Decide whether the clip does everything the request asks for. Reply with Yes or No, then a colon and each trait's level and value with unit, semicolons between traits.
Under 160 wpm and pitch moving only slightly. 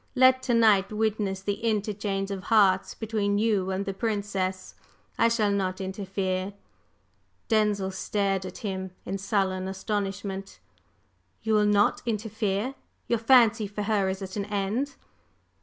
Yes: average, 140 wpm; narrow, 2.2 semitones